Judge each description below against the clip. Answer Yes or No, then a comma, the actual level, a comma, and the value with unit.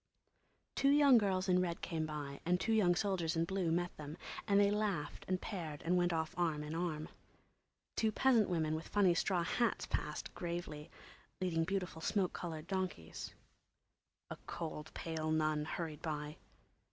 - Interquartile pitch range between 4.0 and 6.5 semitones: No, average, 3.3 semitones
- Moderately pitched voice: Yes, medium, 170 Hz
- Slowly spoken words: No, average, 165 wpm